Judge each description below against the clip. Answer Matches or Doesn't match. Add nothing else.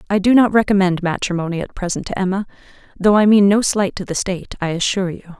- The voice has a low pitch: Doesn't match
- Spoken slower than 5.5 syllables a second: Doesn't match